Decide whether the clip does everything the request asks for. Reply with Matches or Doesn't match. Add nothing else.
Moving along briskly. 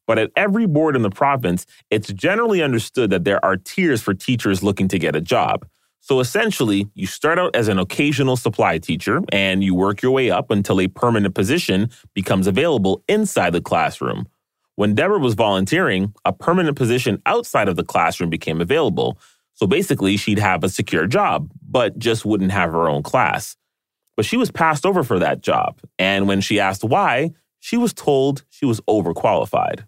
Doesn't match